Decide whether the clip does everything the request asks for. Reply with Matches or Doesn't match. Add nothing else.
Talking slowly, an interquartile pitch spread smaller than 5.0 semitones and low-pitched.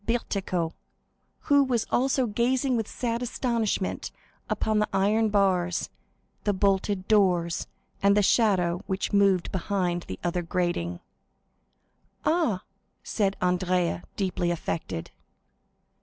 Doesn't match